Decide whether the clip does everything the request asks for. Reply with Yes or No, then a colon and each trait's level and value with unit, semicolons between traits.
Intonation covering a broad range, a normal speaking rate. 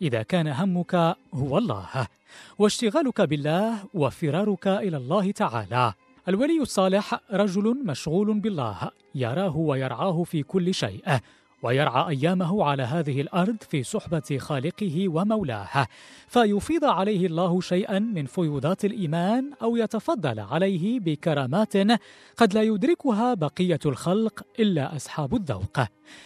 Yes: wide, 6.1 semitones; average, 110 wpm